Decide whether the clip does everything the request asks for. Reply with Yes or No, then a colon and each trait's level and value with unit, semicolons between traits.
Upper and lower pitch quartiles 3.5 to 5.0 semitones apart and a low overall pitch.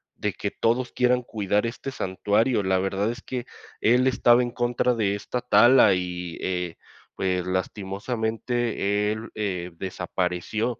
Yes: average, 4.3 semitones; low, 105 Hz